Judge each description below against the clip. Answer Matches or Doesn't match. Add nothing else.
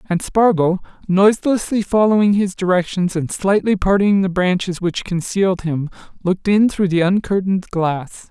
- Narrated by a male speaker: Matches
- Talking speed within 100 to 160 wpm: Matches